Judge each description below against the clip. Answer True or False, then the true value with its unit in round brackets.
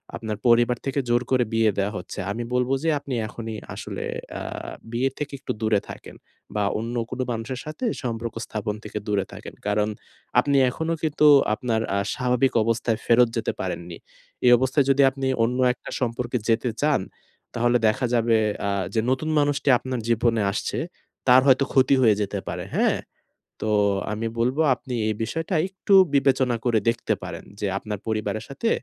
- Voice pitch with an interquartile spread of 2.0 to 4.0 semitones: True (2.9 semitones)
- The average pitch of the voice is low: True (120 Hz)